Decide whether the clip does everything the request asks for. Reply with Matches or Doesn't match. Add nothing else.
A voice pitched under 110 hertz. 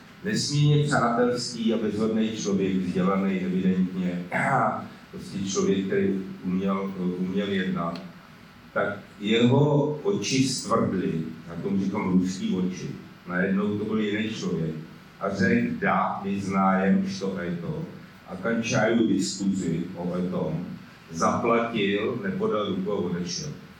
Matches